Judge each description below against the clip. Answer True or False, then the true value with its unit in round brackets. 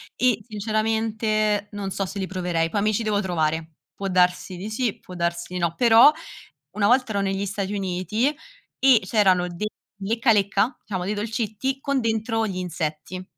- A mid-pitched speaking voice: False (205 Hz)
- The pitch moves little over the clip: False (3.3 semitones)